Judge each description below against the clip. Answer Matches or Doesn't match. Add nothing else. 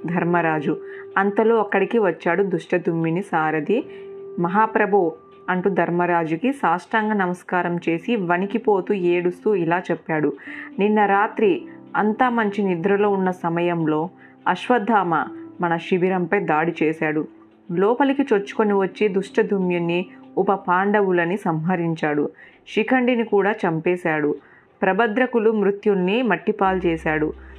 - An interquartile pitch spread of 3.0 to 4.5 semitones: Matches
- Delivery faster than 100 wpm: Doesn't match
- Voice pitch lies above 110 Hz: Matches